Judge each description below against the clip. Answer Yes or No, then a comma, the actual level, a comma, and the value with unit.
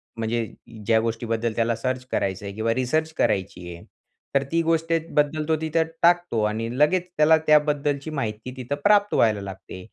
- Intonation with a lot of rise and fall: Yes, wide, 6.0 semitones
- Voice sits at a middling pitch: No, low, 130 Hz